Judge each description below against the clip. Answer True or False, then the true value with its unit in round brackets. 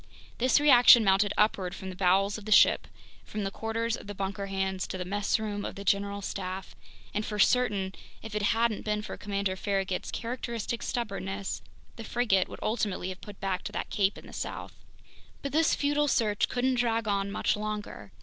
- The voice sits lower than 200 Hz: False (205 Hz)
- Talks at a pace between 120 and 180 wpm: False (190 wpm)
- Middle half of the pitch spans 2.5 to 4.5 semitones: True (2.8 semitones)